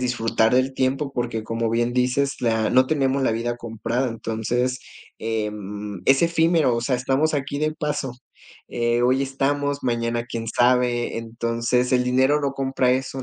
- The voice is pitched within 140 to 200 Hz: No, low, 125 Hz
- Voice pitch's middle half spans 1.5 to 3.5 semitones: Yes, narrow, 2.5 semitones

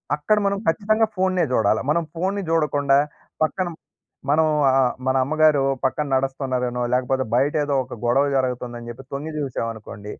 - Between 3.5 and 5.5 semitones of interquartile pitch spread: Yes, average, 4.2 semitones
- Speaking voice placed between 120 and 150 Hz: Yes, low, 135 Hz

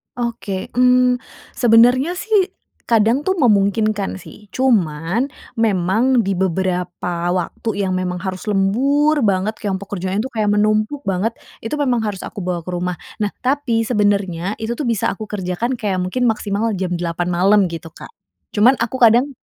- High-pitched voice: Yes, high, 210 Hz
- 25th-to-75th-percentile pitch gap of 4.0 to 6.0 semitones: Yes, average, 4.5 semitones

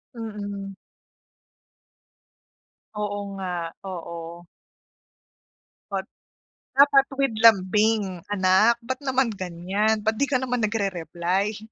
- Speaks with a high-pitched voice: Yes, high, 205 Hz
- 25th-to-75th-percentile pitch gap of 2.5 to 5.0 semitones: Yes, average, 3.4 semitones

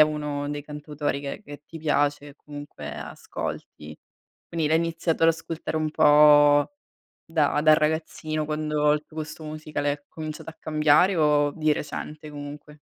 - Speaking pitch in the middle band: Yes, medium, 150 Hz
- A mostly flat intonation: Yes, narrow, 1.2 semitones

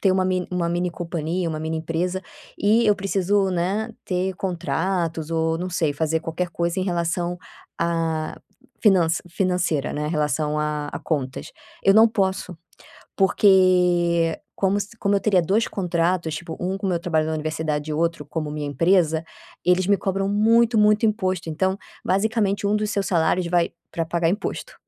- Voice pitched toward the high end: No, medium, 175 Hz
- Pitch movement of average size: Yes, average, 3.1 semitones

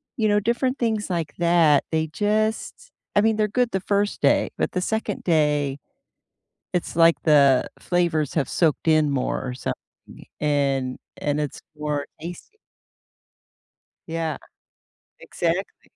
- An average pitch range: No, wide, 5.9 semitones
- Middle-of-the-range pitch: Yes, medium, 165 Hz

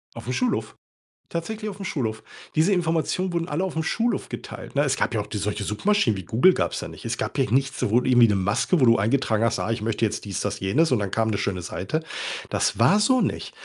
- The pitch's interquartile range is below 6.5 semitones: No, wide, 7.9 semitones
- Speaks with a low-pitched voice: Yes, low, 125 Hz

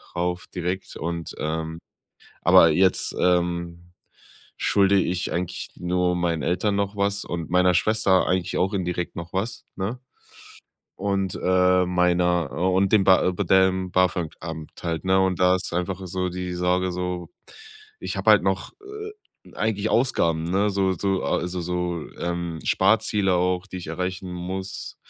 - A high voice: No, very low, 90 Hz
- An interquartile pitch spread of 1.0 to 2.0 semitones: Yes, narrow, 1.5 semitones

